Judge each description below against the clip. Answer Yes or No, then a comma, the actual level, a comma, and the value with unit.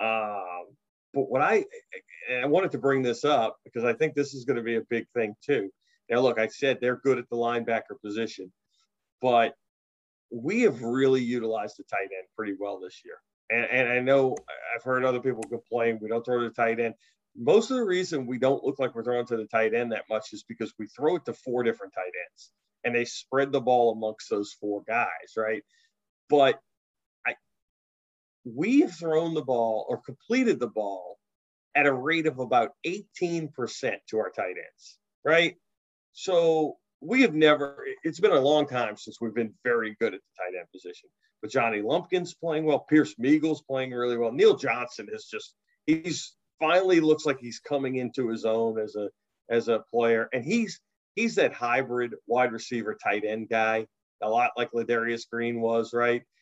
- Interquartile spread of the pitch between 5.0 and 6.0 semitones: Yes, wide, 5.5 semitones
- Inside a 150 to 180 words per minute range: No, average, 190 wpm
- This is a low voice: Yes, low, 125 Hz